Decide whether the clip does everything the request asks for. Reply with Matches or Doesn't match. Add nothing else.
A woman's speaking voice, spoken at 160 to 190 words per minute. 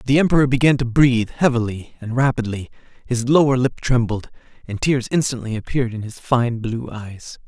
Doesn't match